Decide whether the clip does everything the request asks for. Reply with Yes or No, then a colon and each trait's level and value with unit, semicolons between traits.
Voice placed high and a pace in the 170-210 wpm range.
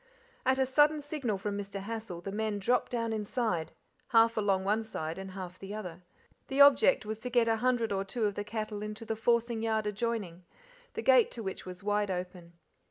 Yes: high, 215 Hz; fast, 205 wpm